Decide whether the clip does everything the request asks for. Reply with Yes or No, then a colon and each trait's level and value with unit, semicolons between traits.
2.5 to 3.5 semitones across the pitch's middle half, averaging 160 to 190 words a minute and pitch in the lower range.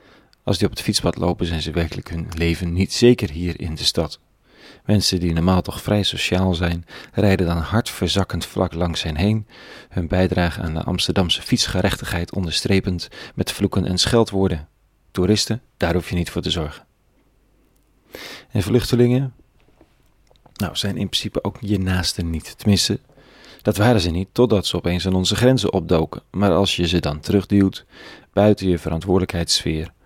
Yes: average, 3.0 semitones; average, 165 wpm; very low, 95 Hz